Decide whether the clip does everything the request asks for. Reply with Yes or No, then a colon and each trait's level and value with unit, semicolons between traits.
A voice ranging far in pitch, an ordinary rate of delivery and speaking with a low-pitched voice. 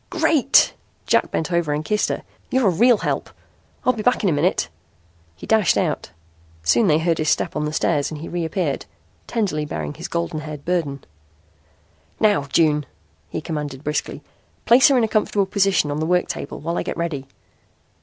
No: wide, 5.7 semitones; average, 185 wpm; medium, 165 Hz